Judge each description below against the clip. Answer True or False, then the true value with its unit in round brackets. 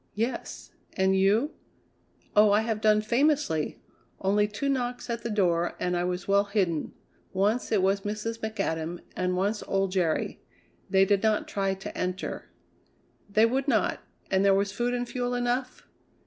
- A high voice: True (205 Hz)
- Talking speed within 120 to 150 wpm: False (160 wpm)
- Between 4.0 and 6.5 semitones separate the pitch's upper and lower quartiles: False (3.2 semitones)